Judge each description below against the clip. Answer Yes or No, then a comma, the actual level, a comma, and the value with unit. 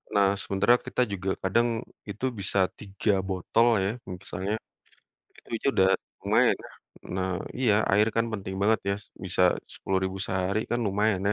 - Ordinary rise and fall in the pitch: No, narrow, 2.3 semitones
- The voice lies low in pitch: Yes, low, 100 Hz